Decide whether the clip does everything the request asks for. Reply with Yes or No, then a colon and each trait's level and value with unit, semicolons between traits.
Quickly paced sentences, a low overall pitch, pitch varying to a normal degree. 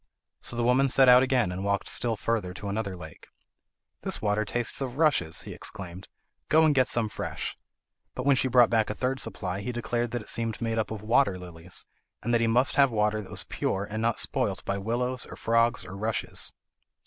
Yes: fast, 215 wpm; low, 115 Hz; average, 3.6 semitones